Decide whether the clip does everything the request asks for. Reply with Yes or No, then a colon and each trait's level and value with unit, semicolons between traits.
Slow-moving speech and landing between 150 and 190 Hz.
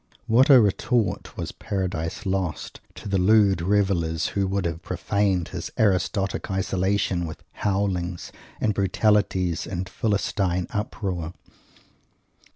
No: slow, 115 wpm; very low, 95 Hz